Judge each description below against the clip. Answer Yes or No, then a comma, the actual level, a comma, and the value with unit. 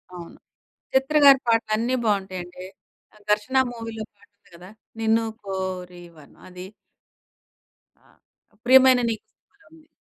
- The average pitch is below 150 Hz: No, high, 215 Hz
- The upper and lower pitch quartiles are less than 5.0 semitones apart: No, average, 5.3 semitones